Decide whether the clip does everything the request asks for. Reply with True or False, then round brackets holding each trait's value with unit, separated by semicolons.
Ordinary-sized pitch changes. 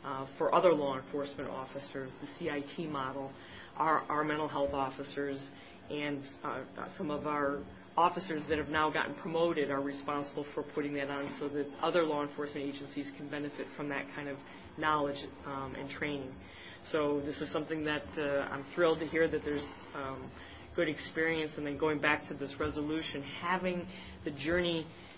False (1.8 semitones)